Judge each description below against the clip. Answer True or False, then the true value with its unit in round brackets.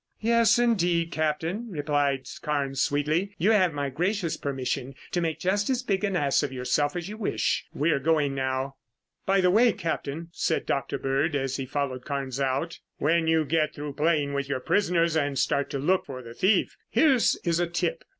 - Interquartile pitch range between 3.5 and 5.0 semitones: True (4.7 semitones)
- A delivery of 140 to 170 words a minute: False (190 wpm)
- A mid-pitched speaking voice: True (155 Hz)